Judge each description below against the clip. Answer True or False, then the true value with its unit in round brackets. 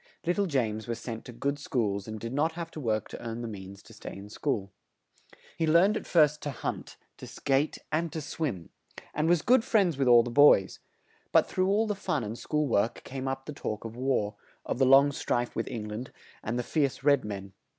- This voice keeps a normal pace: False (225 wpm)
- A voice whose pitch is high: False (135 Hz)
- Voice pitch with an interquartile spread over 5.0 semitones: True (5.4 semitones)